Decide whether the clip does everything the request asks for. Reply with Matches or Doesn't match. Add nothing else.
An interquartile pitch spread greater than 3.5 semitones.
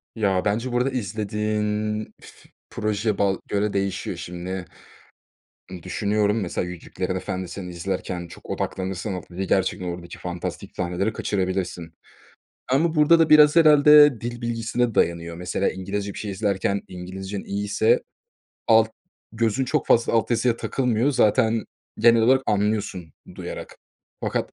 Matches